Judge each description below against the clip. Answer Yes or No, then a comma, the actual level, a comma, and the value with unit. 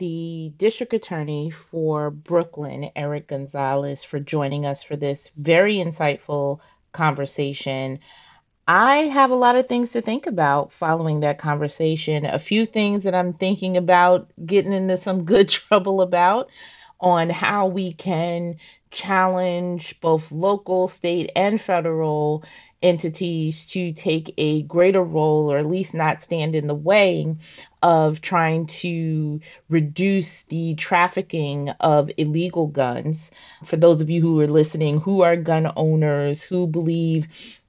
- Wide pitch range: No, average, 3.2 semitones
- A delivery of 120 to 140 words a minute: Yes, slow, 135 wpm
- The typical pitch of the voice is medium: Yes, medium, 165 Hz